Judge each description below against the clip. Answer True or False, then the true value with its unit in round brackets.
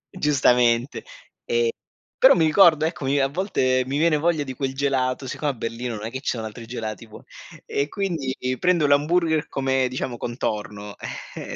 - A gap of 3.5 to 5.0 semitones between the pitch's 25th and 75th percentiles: True (4.4 semitones)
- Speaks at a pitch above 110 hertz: True (135 Hz)